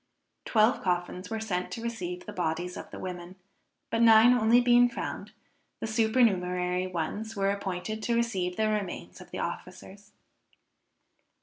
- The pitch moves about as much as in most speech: Yes, average, 3.9 semitones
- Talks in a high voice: Yes, high, 205 Hz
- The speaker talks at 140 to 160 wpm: Yes, average, 145 wpm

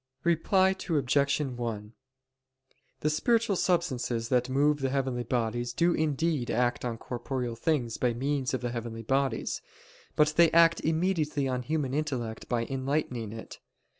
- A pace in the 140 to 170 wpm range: Yes, average, 145 wpm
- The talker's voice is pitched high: No, low, 135 Hz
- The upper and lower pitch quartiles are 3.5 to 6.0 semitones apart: Yes, average, 4.2 semitones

